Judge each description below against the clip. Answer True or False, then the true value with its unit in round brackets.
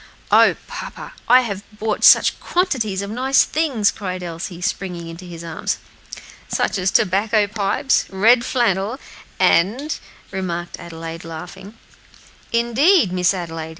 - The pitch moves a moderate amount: True (4.9 semitones)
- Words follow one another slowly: True (130 wpm)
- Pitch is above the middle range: True (195 Hz)